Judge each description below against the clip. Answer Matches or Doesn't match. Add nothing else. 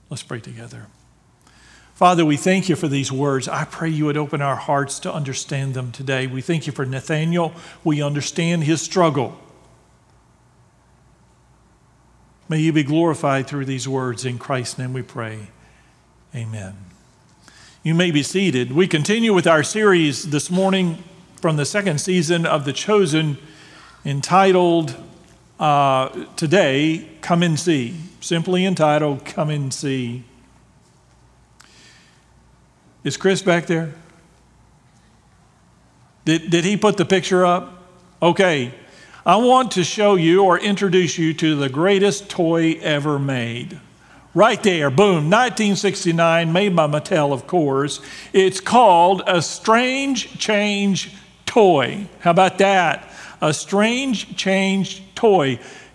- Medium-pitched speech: Matches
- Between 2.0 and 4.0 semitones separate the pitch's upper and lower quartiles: Doesn't match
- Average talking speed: Doesn't match